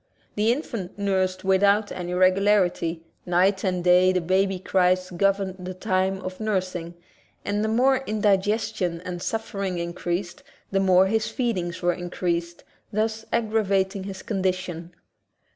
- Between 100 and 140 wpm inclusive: Yes, slow, 135 wpm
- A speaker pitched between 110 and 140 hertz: No, high, 190 Hz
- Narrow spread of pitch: Yes, narrow, 2.2 semitones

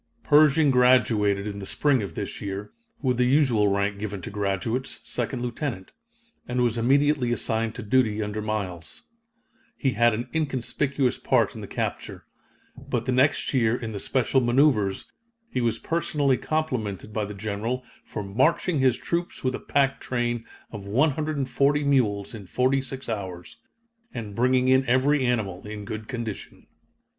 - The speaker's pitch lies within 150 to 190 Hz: No, low, 120 Hz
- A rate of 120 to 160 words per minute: Yes, average, 155 wpm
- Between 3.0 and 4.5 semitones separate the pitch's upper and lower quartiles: Yes, average, 4.2 semitones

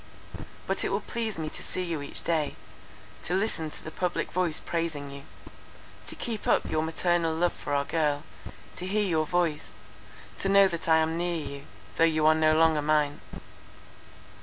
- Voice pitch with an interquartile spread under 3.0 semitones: Yes, narrow, 2.4 semitones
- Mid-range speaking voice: Yes, medium, 160 Hz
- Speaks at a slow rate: No, average, 185 wpm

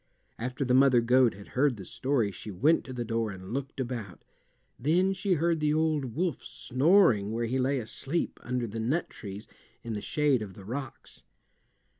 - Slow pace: No, average, 185 wpm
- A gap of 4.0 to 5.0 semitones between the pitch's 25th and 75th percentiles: Yes, average, 4.5 semitones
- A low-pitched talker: Yes, low, 125 Hz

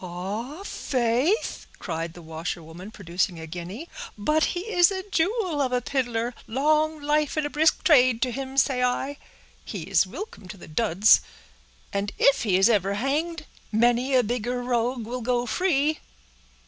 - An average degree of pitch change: No, wide, 6.8 semitones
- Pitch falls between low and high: No, high, 245 Hz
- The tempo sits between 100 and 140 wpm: No, average, 160 wpm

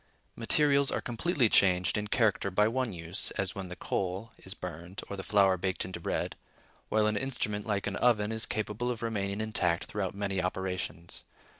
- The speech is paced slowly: No, average, 180 wpm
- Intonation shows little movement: No, average, 3.1 semitones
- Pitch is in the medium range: No, low, 100 Hz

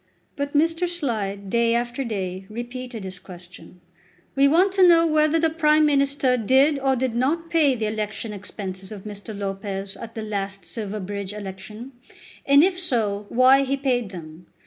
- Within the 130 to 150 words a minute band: No, average, 165 wpm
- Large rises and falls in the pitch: Yes, wide, 5.9 semitones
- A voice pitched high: Yes, high, 235 Hz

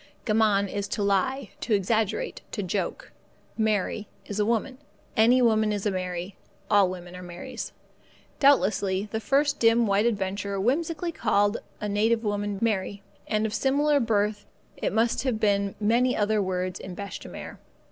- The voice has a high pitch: Yes, high, 210 Hz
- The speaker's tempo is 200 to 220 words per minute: No, average, 155 wpm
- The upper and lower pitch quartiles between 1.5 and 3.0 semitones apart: Yes, narrow, 2.6 semitones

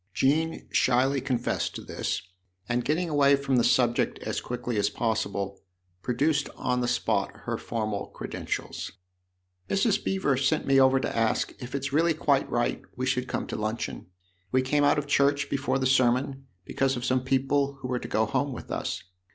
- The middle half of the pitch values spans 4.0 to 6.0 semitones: No, narrow, 2.6 semitones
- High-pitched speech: No, low, 130 Hz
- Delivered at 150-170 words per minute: No, average, 185 wpm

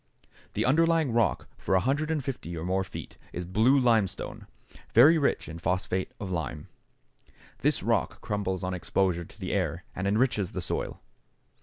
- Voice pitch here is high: No, low, 100 Hz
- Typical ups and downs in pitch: No, wide, 6.0 semitones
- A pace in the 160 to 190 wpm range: No, average, 150 wpm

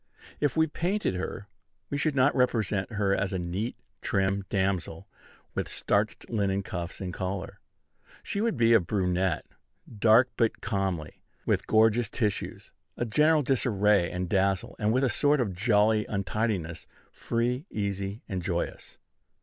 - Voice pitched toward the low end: Yes, low, 105 Hz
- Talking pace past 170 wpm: No, average, 145 wpm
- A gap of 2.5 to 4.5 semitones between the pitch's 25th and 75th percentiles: Yes, average, 3.9 semitones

